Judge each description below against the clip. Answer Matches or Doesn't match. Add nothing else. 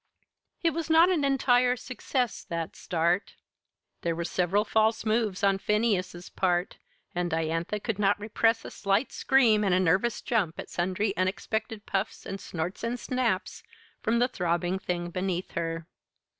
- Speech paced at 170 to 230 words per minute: Doesn't match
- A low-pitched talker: Doesn't match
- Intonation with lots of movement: Doesn't match